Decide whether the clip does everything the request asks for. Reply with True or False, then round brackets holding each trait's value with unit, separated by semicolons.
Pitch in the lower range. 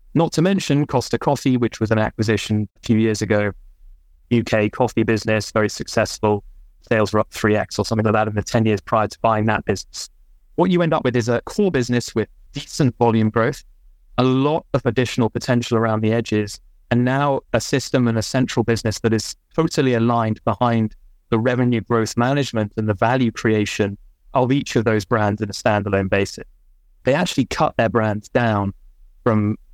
True (115 Hz)